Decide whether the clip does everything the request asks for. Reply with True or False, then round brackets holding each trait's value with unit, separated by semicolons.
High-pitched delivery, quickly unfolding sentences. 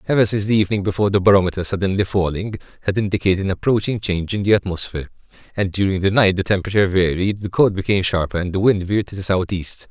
False (95 Hz; 210 wpm)